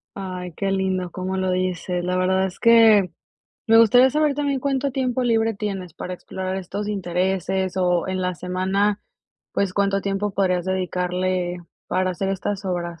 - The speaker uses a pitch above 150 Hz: Yes, high, 190 Hz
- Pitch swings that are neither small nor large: No, narrow, 2.2 semitones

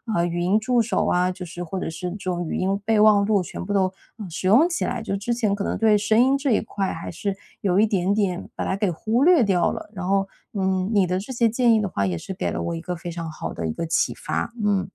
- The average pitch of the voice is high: Yes, high, 195 Hz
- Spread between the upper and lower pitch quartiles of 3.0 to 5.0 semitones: Yes, average, 3.3 semitones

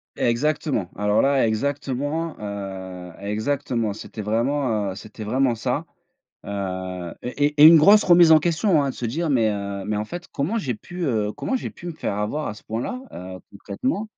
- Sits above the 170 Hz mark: No, low, 120 Hz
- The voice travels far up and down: Yes, wide, 6.7 semitones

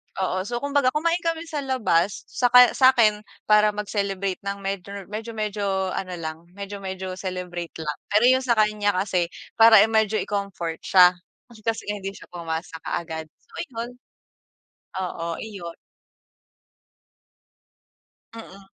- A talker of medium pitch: No, high, 200 Hz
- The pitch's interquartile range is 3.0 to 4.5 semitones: Yes, average, 3.6 semitones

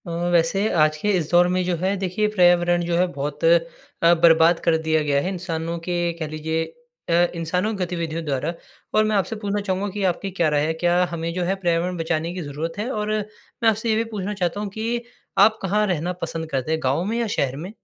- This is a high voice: No, medium, 175 Hz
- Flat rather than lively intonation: No, average, 3.2 semitones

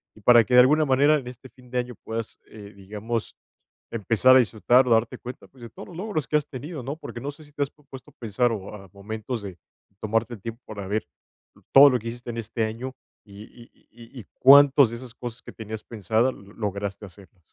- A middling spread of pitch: Yes, average, 3.3 semitones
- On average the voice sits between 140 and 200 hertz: No, low, 120 Hz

